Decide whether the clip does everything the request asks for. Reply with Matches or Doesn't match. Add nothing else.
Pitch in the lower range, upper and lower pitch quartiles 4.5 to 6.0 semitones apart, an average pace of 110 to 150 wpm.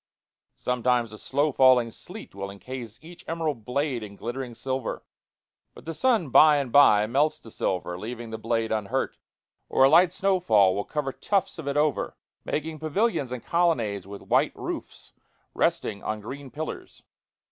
Doesn't match